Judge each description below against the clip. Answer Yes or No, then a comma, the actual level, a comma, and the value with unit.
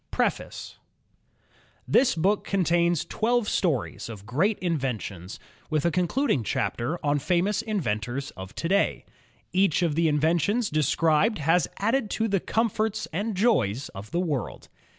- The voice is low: No, medium, 170 Hz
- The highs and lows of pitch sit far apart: Yes, wide, 6.4 semitones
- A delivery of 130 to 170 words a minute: Yes, average, 140 wpm